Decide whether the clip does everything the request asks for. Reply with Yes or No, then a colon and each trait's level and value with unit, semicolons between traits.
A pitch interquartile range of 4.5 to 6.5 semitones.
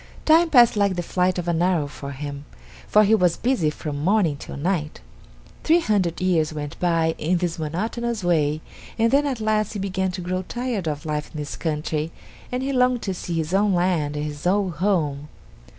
Yes: wide, 5.5 semitones